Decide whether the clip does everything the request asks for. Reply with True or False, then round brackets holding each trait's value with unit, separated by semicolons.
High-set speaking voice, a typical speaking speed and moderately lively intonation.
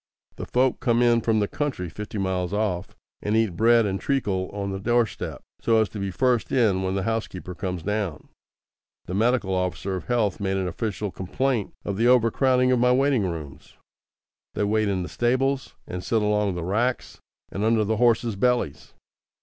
False (105 Hz; 190 wpm; 4.0 semitones)